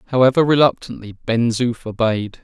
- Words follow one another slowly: Yes, slow, 125 wpm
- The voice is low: Yes, low, 120 Hz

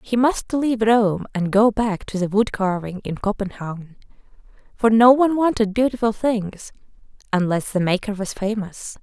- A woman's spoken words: Yes, female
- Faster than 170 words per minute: No, average, 160 wpm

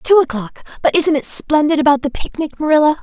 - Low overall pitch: No, very high, 295 Hz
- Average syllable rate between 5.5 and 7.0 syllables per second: Yes, 5.8 syllables/s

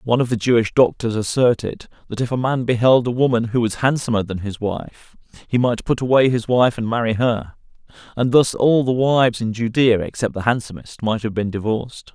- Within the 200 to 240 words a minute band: Yes, fast, 205 wpm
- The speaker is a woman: No, male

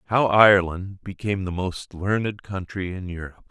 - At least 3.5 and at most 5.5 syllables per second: Yes, 5.3 syllables/s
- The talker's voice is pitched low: Yes, very low, 95 Hz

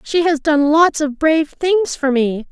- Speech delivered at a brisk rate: Yes, fast, 215 wpm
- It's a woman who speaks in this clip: Yes, female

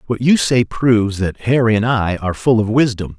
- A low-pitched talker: Yes, low, 110 Hz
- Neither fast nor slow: No, fast, 225 wpm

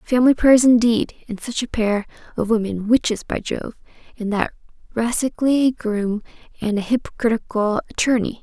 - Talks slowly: Yes, slow, 130 wpm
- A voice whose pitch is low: No, high, 230 Hz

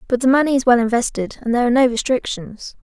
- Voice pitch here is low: No, high, 245 Hz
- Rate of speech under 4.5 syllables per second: No, 6.9 syllables/s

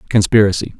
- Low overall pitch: Yes, low, 105 Hz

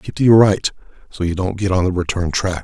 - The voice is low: Yes, very low, 95 Hz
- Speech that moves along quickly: Yes, fast, 275 wpm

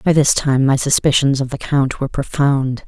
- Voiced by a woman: Yes, female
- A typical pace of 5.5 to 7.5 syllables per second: No, 5.1 syllables/s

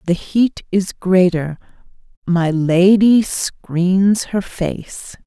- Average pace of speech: No, slow, 105 wpm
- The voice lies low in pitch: No, medium, 185 Hz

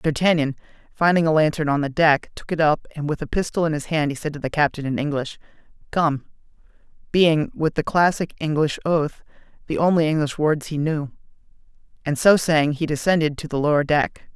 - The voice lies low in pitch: No, medium, 155 Hz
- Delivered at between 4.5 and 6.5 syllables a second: No, 4.3 syllables/s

